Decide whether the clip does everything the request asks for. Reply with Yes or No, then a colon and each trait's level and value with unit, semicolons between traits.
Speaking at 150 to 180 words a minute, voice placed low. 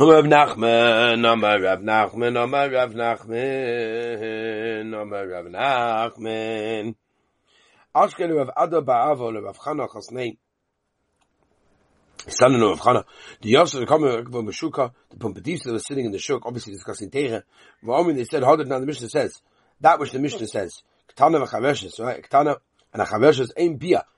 Yes: average, 160 wpm; low, 115 Hz